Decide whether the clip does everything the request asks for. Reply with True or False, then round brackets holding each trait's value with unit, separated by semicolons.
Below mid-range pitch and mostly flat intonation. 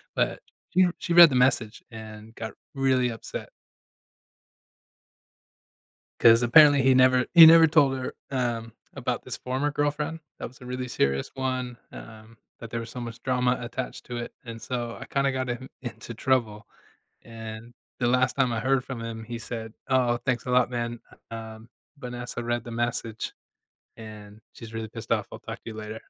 True (120 Hz; 2.3 semitones)